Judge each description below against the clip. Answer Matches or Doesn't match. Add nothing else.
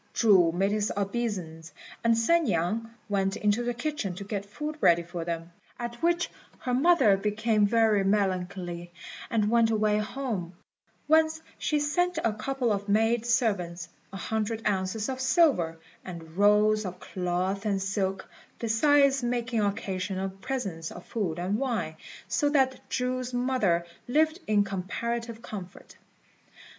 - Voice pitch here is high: Matches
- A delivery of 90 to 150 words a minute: Matches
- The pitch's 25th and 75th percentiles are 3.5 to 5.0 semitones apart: Matches